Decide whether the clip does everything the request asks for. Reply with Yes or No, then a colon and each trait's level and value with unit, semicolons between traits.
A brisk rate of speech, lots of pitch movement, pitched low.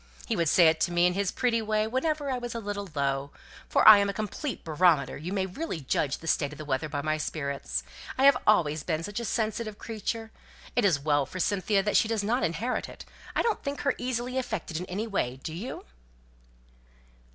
No: fast, 225 wpm; wide, 6.6 semitones; high, 200 Hz